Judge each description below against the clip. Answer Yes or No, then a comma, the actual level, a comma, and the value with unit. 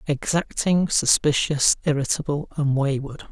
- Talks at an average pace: No, slow, 90 wpm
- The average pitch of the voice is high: No, medium, 145 Hz